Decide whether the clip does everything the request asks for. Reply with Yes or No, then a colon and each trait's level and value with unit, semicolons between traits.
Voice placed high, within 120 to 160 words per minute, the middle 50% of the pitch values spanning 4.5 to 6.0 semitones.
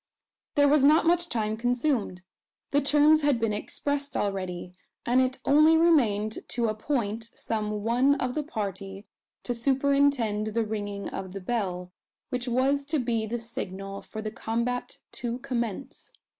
Yes: high, 235 Hz; average, 150 wpm; average, 4.9 semitones